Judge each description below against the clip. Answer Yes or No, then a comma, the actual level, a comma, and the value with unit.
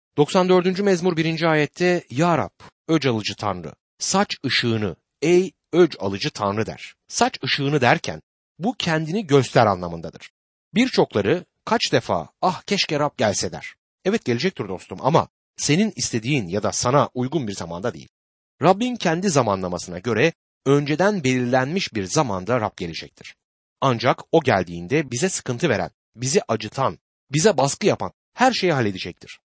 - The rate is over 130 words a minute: Yes, fast, 140 wpm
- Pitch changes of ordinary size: No, wide, 8.3 semitones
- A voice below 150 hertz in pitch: Yes, medium, 140 Hz